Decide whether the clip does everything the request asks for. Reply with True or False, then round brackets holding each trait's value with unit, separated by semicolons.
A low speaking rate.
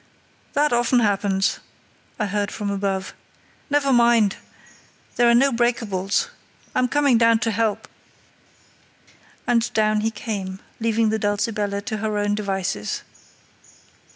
True (125 wpm)